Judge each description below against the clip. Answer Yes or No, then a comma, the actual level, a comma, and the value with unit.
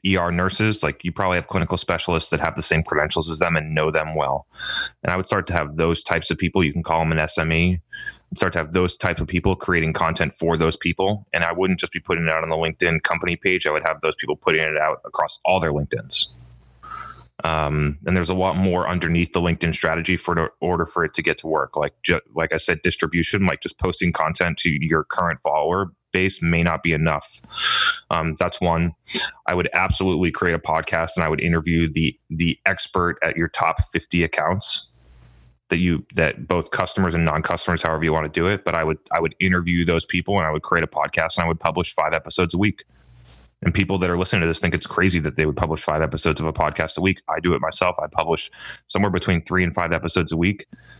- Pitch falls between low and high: No, very low, 85 Hz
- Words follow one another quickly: Yes, fast, 235 wpm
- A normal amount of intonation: No, narrow, 2.2 semitones